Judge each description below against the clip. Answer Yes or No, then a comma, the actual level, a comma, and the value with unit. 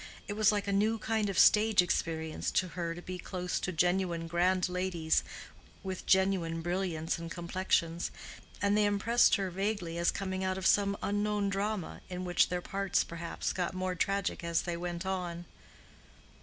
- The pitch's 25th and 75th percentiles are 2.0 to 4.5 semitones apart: Yes, narrow, 2.5 semitones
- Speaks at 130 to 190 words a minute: Yes, average, 170 wpm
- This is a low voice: No, medium, 185 Hz